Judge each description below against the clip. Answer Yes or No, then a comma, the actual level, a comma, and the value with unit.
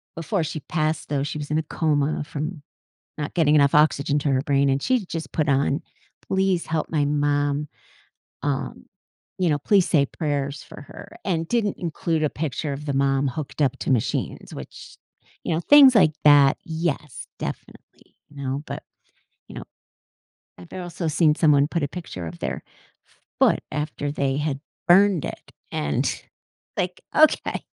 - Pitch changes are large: No, average, 2.9 semitones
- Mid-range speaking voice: Yes, medium, 150 Hz